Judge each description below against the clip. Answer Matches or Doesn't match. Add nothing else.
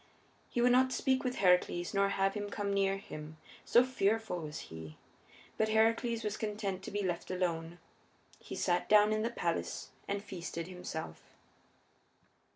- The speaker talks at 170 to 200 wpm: Doesn't match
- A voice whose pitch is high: Matches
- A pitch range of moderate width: Matches